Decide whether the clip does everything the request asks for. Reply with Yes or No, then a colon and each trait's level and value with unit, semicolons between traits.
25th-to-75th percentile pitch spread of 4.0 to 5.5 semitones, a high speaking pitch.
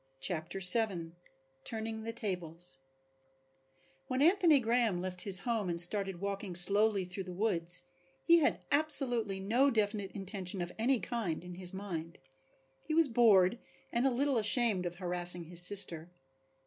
Yes: average, 4.6 semitones; high, 200 Hz